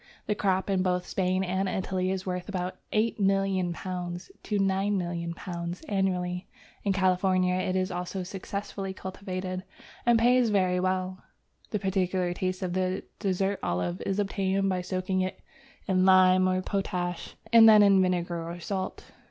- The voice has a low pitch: No, medium, 185 Hz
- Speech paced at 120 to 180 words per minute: Yes, average, 145 wpm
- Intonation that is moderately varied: No, narrow, 1.3 semitones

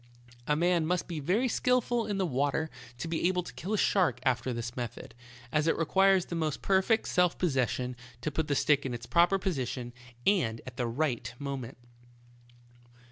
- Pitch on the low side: No, medium, 155 Hz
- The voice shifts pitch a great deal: Yes, wide, 6.1 semitones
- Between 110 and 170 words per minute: No, average, 190 wpm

